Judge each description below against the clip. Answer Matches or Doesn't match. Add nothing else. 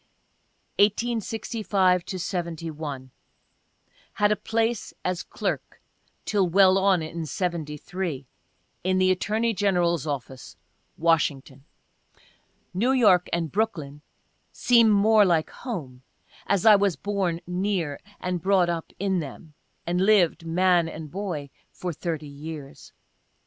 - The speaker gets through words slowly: Matches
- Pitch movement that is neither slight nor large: Matches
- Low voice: Doesn't match